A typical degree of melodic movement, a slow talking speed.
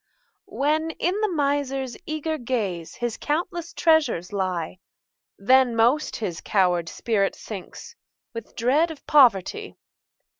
No: wide, 7.8 semitones; slow, 110 wpm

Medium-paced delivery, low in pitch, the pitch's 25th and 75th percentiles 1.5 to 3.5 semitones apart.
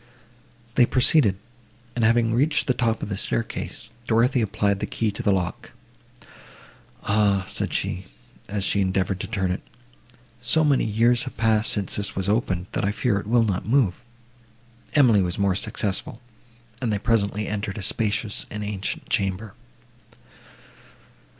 Yes: average, 155 wpm; low, 105 Hz; average, 2.8 semitones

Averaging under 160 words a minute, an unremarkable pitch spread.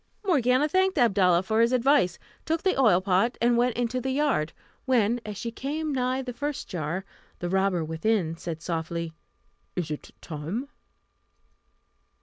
No: average, 150 wpm; wide, 6.9 semitones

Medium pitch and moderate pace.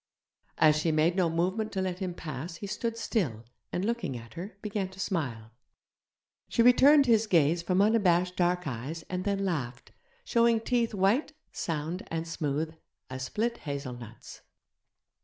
Yes: medium, 180 Hz; average, 155 wpm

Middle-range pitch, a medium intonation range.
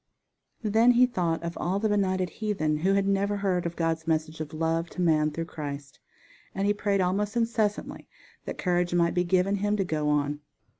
Yes: medium, 180 Hz; average, 3.8 semitones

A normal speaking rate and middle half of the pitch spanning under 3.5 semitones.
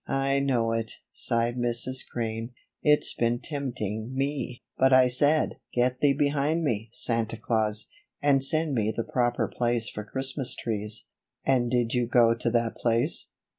Yes: average, 160 wpm; average, 2.9 semitones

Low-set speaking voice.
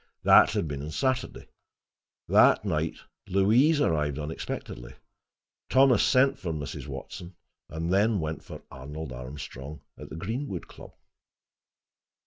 Yes: very low, 80 Hz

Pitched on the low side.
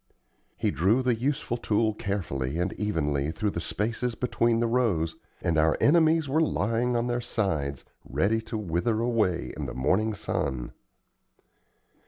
Yes: low, 110 Hz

